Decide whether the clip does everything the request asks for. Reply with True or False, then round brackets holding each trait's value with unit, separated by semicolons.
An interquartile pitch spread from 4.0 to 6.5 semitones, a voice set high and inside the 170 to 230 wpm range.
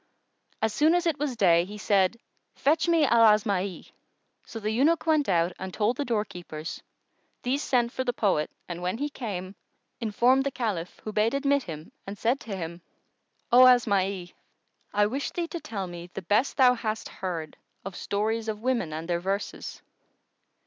True (5.4 semitones; 215 Hz; 175 wpm)